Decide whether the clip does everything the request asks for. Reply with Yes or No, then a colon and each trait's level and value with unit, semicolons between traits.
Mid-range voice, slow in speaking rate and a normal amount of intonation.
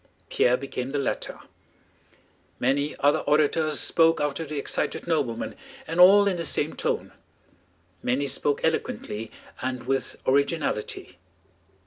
Yes: medium, 145 Hz; slow, 120 wpm; average, 3.7 semitones